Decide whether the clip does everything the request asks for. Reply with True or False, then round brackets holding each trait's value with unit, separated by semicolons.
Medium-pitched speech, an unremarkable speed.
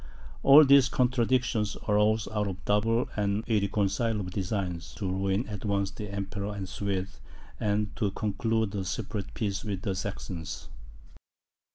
False (105 Hz; 150 wpm)